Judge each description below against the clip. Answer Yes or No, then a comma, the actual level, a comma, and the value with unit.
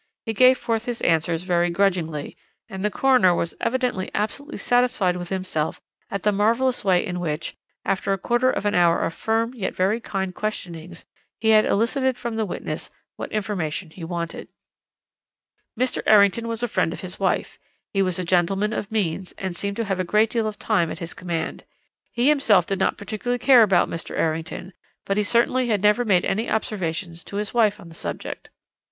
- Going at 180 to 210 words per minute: Yes, average, 195 wpm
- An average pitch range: Yes, average, 4.3 semitones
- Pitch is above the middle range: Yes, high, 200 Hz